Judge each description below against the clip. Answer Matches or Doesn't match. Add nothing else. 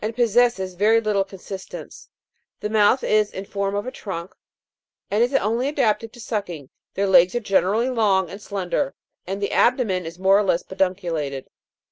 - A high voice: Matches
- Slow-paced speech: Doesn't match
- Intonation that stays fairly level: Doesn't match